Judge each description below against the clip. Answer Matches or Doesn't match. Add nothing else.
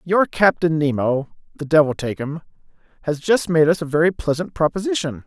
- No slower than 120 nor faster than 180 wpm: Matches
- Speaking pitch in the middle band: Matches